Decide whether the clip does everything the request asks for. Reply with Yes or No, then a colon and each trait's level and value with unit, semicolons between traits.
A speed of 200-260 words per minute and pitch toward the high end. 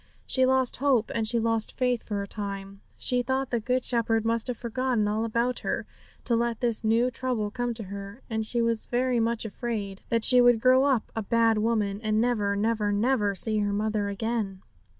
Yes: fast, 205 wpm; high, 230 Hz